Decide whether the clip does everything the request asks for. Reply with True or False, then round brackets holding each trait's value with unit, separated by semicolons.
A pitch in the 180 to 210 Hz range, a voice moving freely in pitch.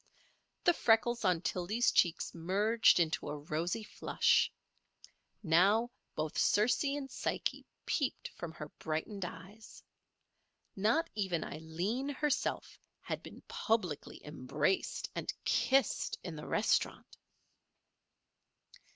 True (190 Hz; 6.1 semitones)